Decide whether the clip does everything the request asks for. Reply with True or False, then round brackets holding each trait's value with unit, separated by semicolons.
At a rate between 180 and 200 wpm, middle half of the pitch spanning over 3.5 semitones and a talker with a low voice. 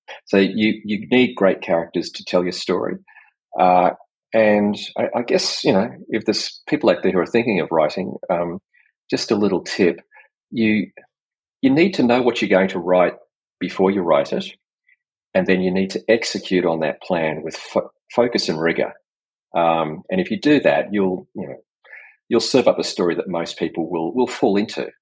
False (195 wpm; 3.2 semitones; 95 Hz)